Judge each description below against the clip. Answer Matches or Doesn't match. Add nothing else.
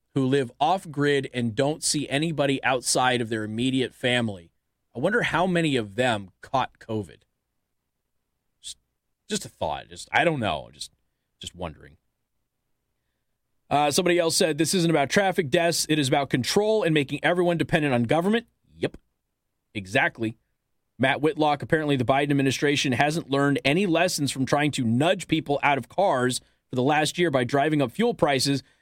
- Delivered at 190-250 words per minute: Doesn't match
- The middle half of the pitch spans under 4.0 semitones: Doesn't match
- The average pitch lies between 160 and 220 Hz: Doesn't match